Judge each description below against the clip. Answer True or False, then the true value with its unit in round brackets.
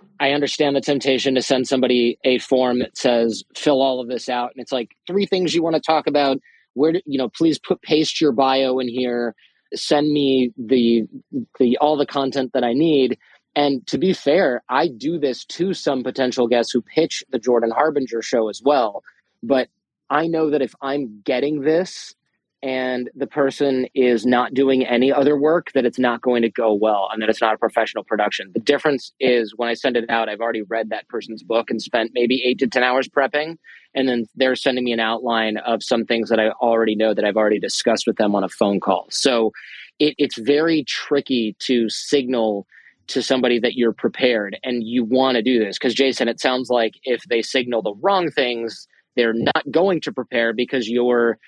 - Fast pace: True (210 wpm)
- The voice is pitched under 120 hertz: False (125 Hz)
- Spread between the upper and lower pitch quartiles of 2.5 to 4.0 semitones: True (3.3 semitones)